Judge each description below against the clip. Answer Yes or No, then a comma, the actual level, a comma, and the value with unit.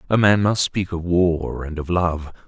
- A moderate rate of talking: No, fast, 220 wpm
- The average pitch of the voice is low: Yes, very low, 90 Hz